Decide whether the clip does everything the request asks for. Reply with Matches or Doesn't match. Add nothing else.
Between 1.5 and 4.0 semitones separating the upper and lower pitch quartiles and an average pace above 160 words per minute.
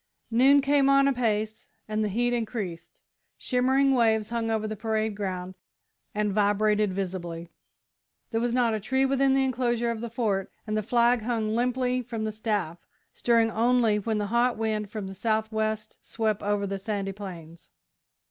Matches